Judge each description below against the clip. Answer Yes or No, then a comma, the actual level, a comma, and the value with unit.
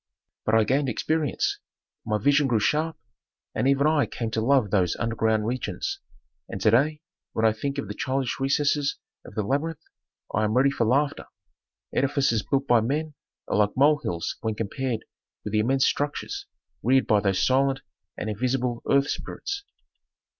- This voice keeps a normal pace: Yes, average, 170 wpm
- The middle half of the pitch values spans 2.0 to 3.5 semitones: No, average, 4.3 semitones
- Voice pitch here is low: Yes, low, 130 Hz